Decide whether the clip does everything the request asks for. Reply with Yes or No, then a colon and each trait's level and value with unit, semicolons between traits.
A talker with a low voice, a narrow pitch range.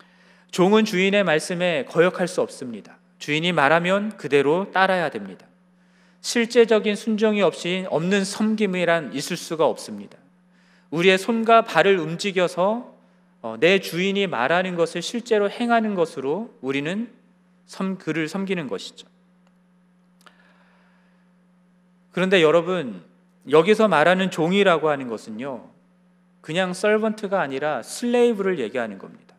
No: medium, 185 Hz; narrow, 2.2 semitones